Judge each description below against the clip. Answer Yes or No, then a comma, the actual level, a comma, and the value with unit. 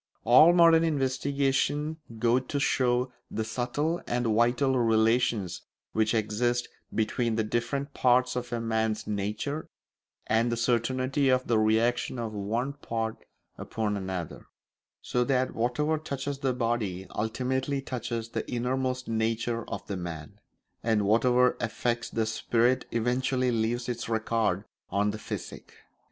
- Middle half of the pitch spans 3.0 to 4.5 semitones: No, narrow, 2.6 semitones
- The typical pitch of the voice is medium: No, low, 120 Hz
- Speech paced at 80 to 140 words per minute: Yes, slow, 135 wpm